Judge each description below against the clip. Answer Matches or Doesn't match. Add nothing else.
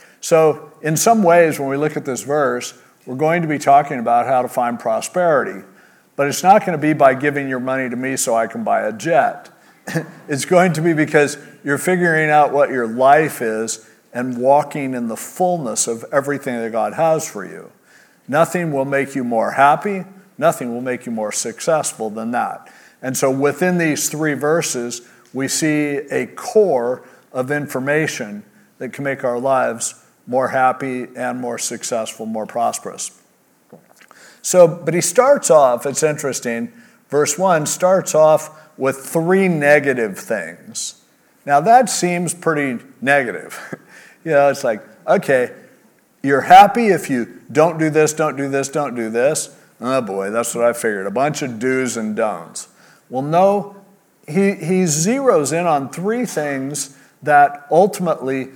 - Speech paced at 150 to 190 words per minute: Matches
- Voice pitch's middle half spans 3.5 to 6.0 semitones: Matches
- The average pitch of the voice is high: Doesn't match